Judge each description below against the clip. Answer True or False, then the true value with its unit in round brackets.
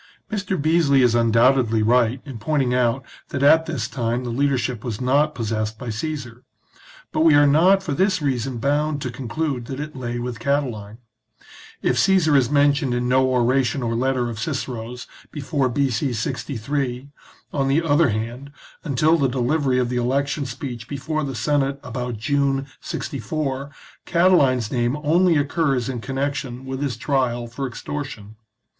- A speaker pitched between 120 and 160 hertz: True (135 Hz)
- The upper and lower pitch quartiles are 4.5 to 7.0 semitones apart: False (3.1 semitones)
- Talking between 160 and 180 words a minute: True (165 wpm)